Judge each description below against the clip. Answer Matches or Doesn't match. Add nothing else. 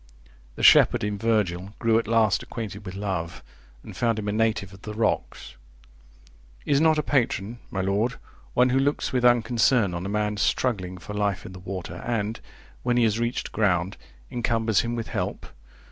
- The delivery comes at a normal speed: Matches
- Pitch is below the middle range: Matches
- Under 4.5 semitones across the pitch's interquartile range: Matches